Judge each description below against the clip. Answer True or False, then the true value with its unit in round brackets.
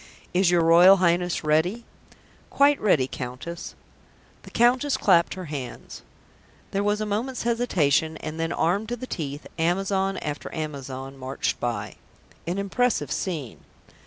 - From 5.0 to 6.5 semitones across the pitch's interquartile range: True (5.3 semitones)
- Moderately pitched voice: True (175 Hz)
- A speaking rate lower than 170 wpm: True (135 wpm)